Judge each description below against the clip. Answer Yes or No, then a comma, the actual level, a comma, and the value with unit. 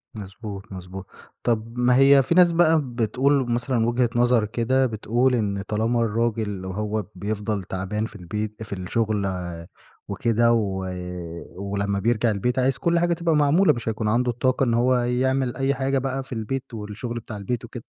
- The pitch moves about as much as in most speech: Yes, average, 3.6 semitones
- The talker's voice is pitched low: Yes, low, 115 Hz